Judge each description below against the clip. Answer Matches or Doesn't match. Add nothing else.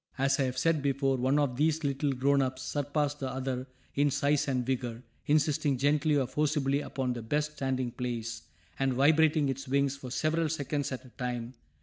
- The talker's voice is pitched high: Doesn't match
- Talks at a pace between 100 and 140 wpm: Doesn't match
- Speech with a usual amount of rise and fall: Doesn't match